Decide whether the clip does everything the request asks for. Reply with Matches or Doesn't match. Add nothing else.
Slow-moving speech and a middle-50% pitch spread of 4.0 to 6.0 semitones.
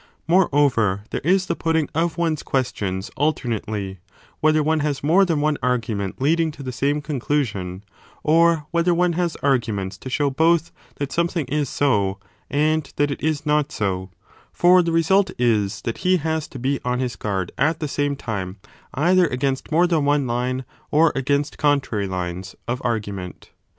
Doesn't match